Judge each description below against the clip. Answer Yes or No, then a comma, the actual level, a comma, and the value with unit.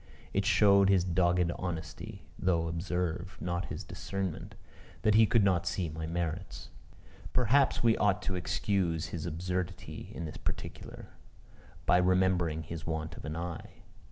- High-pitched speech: No, very low, 90 Hz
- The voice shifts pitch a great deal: No, narrow, 2.5 semitones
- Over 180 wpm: No, average, 145 wpm